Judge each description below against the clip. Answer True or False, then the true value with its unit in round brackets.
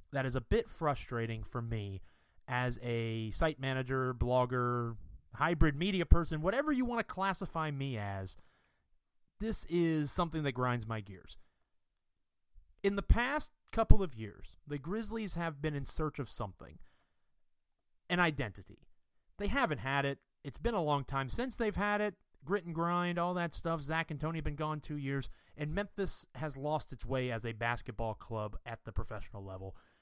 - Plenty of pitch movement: True (7.1 semitones)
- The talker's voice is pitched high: False (135 Hz)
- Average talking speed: True (170 wpm)